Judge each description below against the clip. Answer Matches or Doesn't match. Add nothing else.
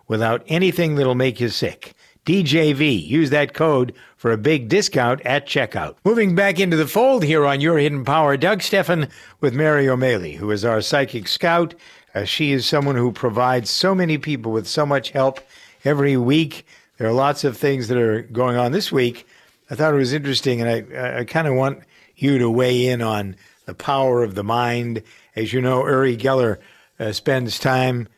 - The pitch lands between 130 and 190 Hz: Matches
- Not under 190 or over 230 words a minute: Matches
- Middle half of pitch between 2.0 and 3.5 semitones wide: Doesn't match